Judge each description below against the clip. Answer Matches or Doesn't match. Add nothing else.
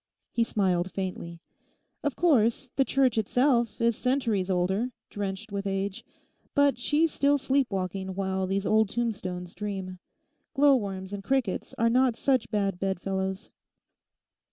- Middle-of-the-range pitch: Doesn't match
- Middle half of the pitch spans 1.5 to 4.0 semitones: Doesn't match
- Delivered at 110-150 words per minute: Matches